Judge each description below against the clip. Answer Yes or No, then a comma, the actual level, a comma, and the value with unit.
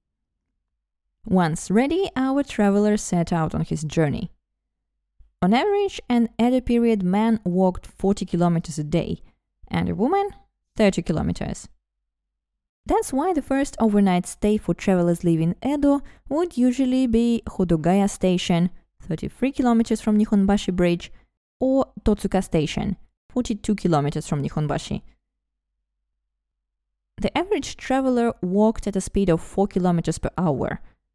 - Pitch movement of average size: No, wide, 7.1 semitones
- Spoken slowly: Yes, slow, 125 wpm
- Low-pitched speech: No, high, 190 Hz